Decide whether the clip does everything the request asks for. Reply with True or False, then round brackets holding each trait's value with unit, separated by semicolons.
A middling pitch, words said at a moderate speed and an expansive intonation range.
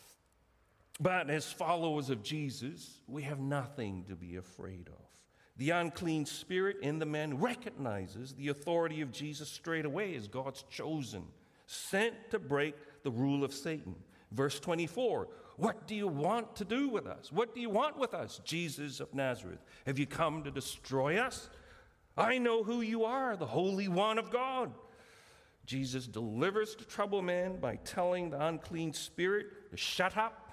True (155 Hz; 165 wpm; 6.5 semitones)